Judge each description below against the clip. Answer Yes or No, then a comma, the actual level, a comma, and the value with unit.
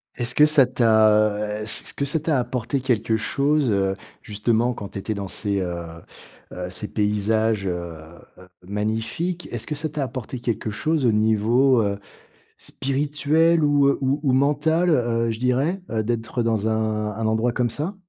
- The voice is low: Yes, low, 115 Hz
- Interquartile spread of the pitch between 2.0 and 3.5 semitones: No, average, 4.7 semitones